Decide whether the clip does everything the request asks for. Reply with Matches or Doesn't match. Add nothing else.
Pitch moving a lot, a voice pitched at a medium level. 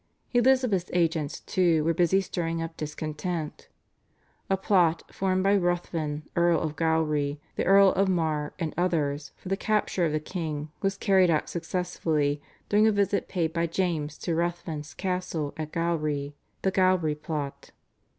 Doesn't match